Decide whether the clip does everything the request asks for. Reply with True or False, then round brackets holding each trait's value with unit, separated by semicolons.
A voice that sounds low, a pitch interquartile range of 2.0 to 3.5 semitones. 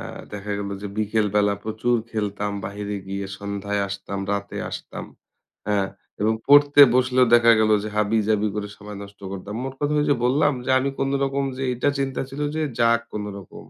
False (105 Hz; 4.3 semitones)